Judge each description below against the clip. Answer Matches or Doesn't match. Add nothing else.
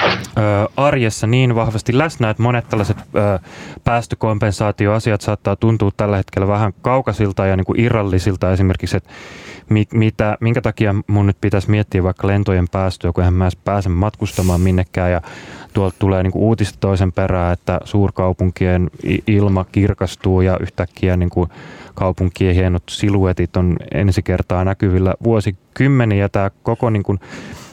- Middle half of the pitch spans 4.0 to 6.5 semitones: Doesn't match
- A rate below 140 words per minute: Doesn't match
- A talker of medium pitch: Doesn't match